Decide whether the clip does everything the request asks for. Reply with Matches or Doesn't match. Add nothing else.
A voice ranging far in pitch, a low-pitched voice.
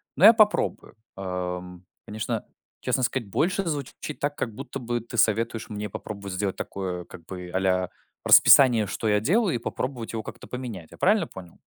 Matches